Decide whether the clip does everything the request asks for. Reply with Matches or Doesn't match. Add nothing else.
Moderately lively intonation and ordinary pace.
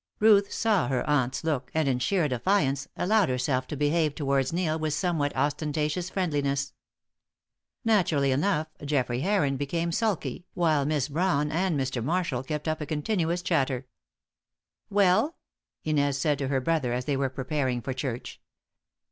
Matches